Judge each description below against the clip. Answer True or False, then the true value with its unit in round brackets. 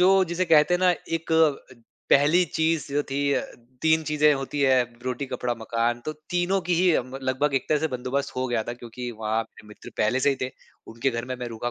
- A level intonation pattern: False (4.5 semitones)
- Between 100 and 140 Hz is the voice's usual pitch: True (135 Hz)